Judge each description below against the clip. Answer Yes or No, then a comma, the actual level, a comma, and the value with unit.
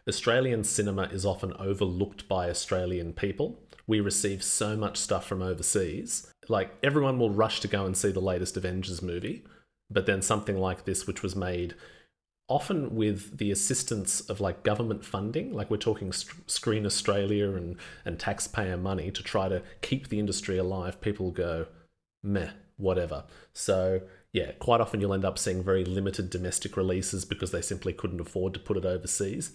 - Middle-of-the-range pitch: No, low, 100 Hz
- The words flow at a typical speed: Yes, average, 170 wpm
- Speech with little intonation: Yes, narrow, 2.3 semitones